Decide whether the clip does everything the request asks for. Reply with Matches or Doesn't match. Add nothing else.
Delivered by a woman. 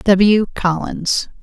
Matches